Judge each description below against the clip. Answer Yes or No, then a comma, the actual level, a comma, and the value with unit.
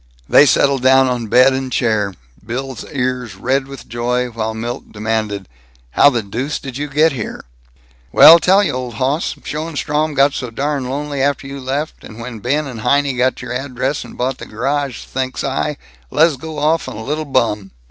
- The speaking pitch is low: Yes, low, 130 Hz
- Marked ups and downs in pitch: No, average, 3.0 semitones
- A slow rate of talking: No, average, 190 wpm